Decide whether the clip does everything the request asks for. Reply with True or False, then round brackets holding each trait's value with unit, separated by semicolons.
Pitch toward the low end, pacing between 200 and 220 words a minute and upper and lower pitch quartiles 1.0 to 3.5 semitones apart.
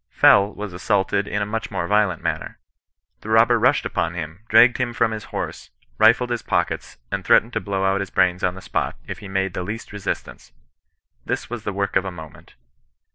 True (100 Hz; 205 wpm; 3.1 semitones)